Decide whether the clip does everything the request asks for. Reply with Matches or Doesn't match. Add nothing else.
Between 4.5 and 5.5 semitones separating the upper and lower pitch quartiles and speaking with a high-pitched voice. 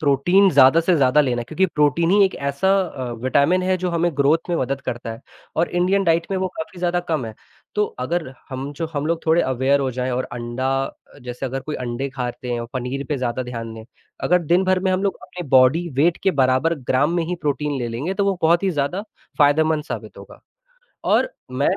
Doesn't match